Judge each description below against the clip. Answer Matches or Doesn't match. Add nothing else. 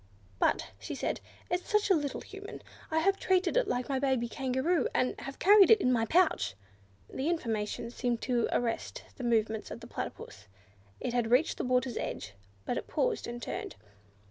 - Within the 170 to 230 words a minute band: Matches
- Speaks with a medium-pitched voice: Doesn't match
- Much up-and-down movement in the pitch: Matches